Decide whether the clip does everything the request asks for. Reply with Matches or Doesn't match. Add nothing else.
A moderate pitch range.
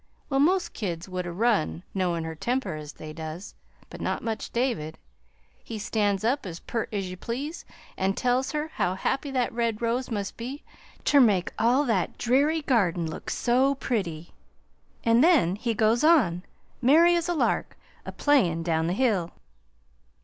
Doesn't match